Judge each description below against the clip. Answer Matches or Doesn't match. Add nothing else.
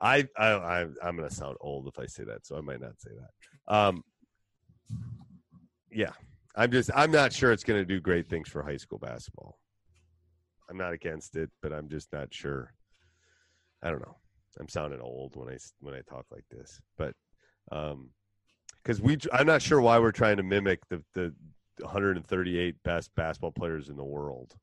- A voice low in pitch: Matches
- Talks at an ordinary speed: Matches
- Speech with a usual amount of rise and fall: Doesn't match